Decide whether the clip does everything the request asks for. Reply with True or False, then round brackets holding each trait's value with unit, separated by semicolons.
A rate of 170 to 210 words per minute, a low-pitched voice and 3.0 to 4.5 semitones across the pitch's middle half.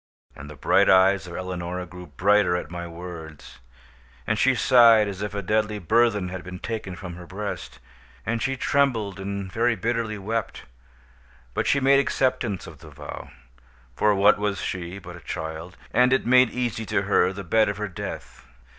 True (180 wpm; 100 Hz; 4.0 semitones)